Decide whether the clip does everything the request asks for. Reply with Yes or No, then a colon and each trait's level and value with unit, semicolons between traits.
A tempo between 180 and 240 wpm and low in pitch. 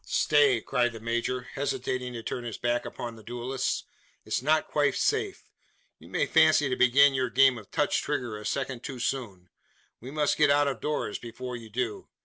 Yes: average, 190 wpm; low, 125 Hz